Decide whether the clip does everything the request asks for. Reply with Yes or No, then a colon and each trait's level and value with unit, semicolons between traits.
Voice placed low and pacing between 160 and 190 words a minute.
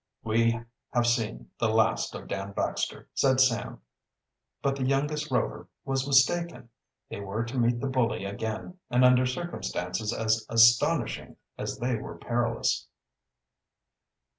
No: low, 120 Hz; slow, 135 wpm